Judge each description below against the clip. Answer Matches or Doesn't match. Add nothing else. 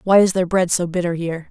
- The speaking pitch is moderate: Matches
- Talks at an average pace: Doesn't match